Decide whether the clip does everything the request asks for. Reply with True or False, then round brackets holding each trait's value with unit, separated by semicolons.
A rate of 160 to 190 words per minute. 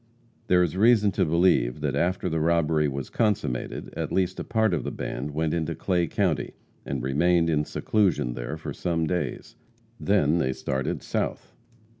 True (170 wpm)